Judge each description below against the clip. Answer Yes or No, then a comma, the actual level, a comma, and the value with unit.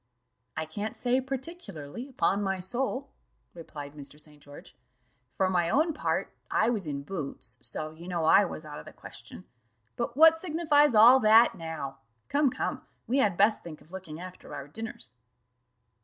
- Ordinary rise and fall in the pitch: No, wide, 8.5 semitones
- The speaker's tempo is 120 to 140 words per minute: No, average, 170 wpm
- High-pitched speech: Yes, high, 195 Hz